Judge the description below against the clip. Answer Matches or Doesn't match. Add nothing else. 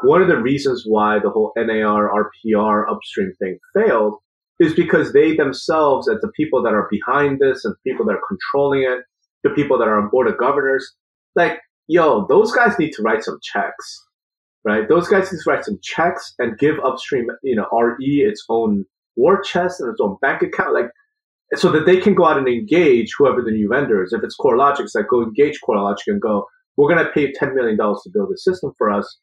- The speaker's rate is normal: Doesn't match